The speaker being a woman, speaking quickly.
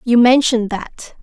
No: female; average, 145 wpm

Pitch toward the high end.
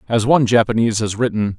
No: low, 115 Hz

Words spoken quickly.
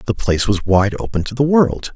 Yes: fast, 245 wpm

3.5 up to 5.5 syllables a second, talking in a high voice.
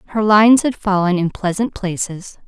Yes: 5.2 syllables/s; high, 200 Hz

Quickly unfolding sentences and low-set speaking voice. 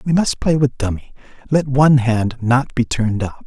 Yes: fast, 210 wpm; low, 130 Hz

